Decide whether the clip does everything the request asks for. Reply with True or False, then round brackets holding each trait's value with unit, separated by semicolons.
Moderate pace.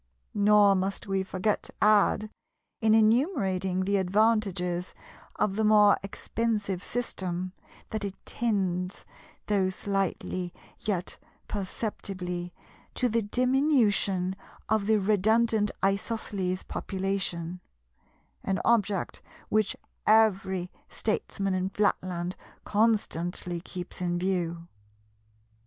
False (95 wpm)